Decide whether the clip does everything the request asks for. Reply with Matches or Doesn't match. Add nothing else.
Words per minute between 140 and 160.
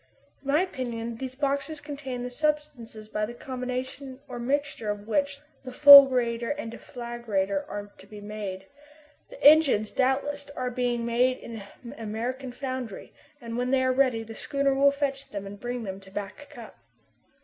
Doesn't match